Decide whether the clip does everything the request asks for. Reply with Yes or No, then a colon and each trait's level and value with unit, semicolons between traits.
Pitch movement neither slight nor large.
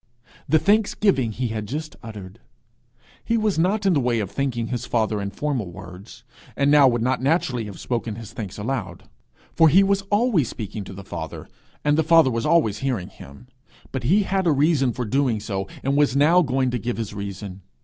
No: wide, 6.4 semitones